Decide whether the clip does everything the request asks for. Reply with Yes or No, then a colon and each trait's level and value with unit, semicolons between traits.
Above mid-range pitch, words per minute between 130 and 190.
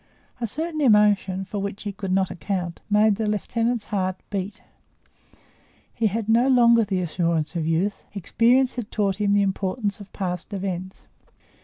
Yes: high, 200 Hz; average, 160 wpm